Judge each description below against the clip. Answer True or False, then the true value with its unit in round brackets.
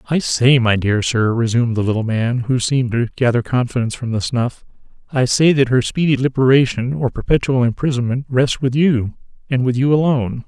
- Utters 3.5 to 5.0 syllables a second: False (5.6 syllables/s)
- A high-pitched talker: False (125 Hz)